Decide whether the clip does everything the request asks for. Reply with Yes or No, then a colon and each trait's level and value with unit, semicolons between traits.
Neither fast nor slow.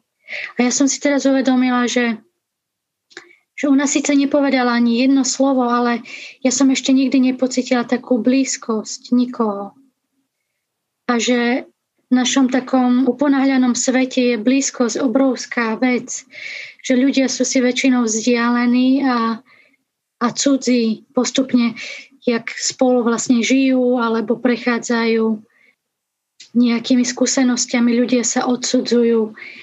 No: slow, 110 wpm